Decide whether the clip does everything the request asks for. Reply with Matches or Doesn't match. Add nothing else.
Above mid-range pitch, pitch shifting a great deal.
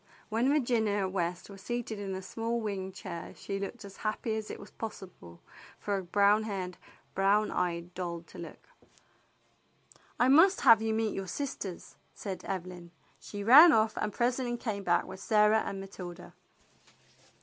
Doesn't match